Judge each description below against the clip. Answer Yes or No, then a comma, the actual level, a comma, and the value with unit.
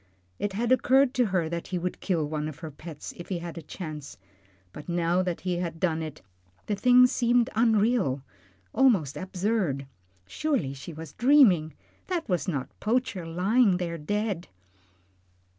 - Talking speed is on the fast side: No, average, 160 wpm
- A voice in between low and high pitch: Yes, medium, 180 Hz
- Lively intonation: Yes, wide, 6.0 semitones